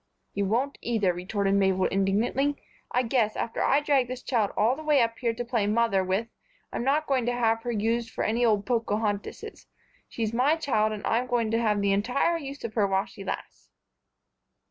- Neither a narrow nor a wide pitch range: Yes, average, 3.4 semitones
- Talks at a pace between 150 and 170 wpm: No, average, 200 wpm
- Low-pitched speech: No, high, 230 Hz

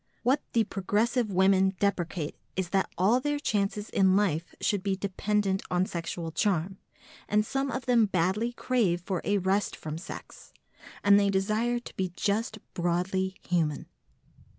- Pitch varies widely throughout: No, average, 2.8 semitones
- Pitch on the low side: No, high, 195 Hz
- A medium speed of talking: Yes, average, 150 wpm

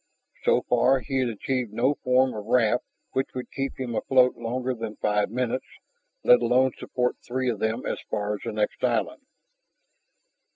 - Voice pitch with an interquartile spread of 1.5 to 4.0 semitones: Yes, narrow, 2.5 semitones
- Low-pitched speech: Yes, low, 125 Hz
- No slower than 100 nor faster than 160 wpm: No, average, 170 wpm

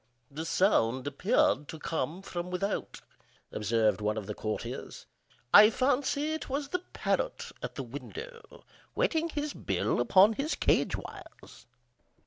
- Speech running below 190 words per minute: Yes, slow, 135 wpm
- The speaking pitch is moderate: No, high, 195 Hz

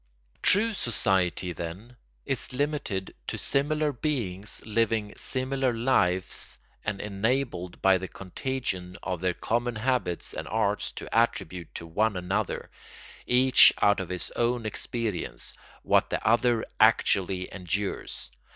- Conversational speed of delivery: No, slow, 125 wpm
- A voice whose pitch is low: Yes, low, 105 Hz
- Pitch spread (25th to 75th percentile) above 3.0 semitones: Yes, average, 5.2 semitones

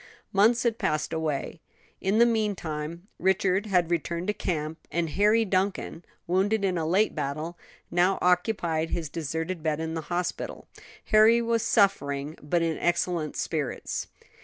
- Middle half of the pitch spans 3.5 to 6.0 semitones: Yes, average, 3.8 semitones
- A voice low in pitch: No, medium, 175 Hz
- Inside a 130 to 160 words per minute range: Yes, average, 145 wpm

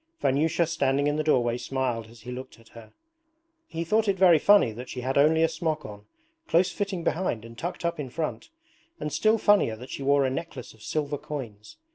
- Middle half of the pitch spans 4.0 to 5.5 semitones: Yes, average, 5.2 semitones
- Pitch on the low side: No, medium, 145 Hz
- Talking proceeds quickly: Yes, fast, 210 wpm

